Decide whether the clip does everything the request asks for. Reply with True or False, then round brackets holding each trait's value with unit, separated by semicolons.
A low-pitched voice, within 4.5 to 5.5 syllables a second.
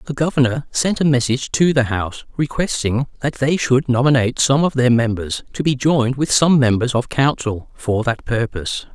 True (130 Hz; 5.2 syllables/s)